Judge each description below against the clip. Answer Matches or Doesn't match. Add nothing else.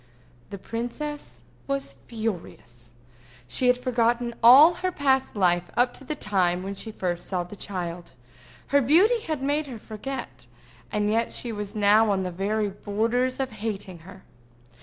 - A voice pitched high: Matches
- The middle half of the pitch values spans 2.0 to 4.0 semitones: Doesn't match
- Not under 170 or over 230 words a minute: Doesn't match